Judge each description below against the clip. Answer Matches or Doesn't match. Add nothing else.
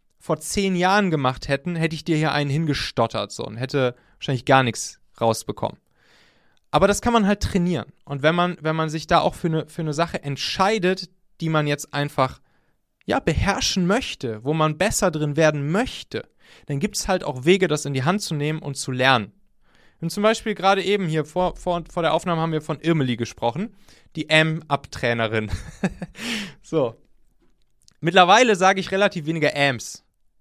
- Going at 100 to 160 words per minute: Doesn't match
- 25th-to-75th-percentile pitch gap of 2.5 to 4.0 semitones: Doesn't match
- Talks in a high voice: Doesn't match